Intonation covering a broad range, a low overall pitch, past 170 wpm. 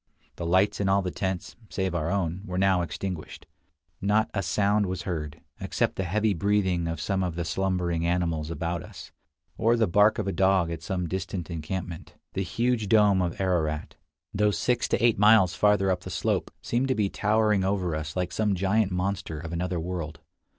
No: average, 3.0 semitones; very low, 95 Hz; average, 190 wpm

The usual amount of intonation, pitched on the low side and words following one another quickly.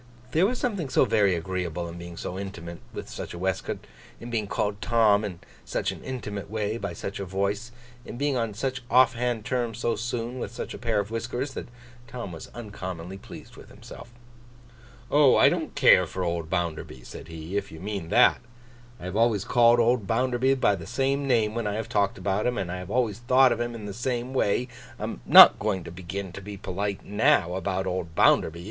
Yes: average, 4.3 semitones; low, 105 Hz; fast, 215 wpm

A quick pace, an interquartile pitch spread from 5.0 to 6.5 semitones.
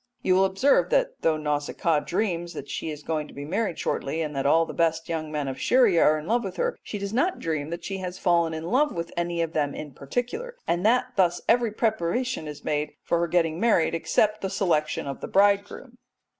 Yes: fast, 235 wpm; average, 5.3 semitones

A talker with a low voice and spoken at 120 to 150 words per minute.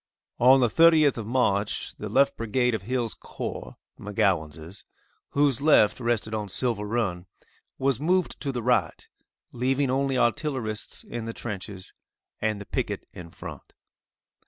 Yes: low, 120 Hz; average, 140 wpm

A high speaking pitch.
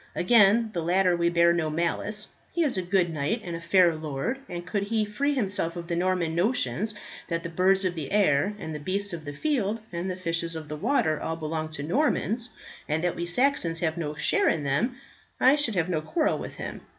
No: medium, 175 Hz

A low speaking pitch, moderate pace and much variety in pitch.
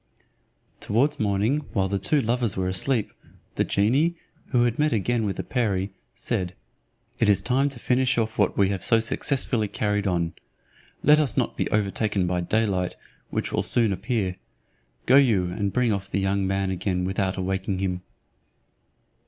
No: low, 105 Hz; average, 170 wpm; average, 4.0 semitones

